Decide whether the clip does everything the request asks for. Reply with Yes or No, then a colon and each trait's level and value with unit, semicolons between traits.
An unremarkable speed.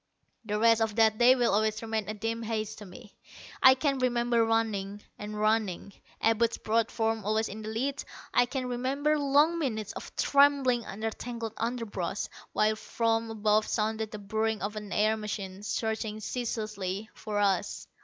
Yes: average, 165 wpm